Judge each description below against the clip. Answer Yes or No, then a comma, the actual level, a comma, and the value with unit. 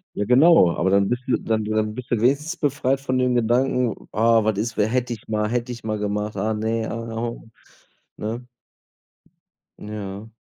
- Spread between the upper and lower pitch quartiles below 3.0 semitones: Yes, narrow, 2.6 semitones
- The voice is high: No, low, 115 Hz